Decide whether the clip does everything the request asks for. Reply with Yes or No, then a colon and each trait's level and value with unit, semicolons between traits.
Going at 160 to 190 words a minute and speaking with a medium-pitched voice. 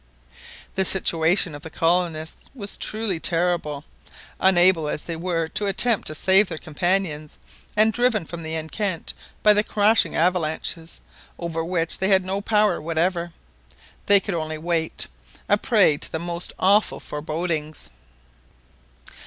No: average, 140 wpm; medium, 175 Hz